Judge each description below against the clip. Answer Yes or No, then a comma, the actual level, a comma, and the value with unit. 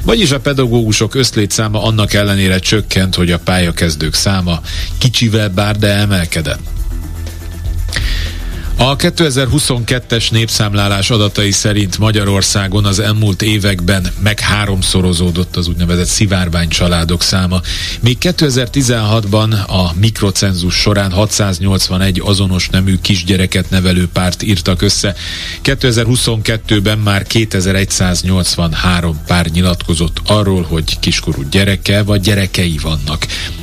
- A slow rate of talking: Yes, slow, 100 wpm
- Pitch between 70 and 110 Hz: Yes, very low, 95 Hz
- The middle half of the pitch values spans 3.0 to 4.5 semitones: Yes, average, 3.5 semitones